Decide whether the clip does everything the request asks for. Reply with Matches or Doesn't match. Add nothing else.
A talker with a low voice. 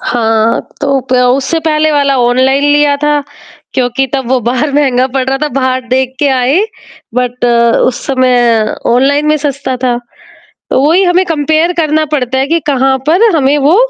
Doesn't match